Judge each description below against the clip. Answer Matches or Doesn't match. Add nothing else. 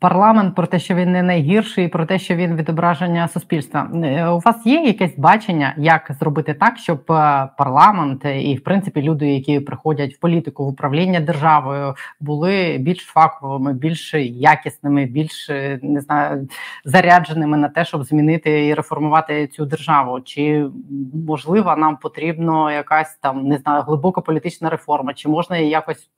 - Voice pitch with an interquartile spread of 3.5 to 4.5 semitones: Doesn't match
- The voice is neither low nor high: Matches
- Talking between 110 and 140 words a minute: Doesn't match